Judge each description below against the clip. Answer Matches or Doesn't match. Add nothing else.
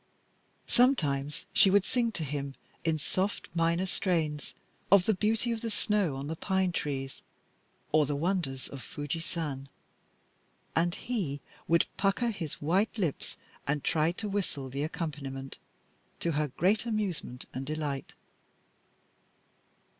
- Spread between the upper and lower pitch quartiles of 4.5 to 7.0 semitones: Matches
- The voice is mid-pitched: Matches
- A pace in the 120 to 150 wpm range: Matches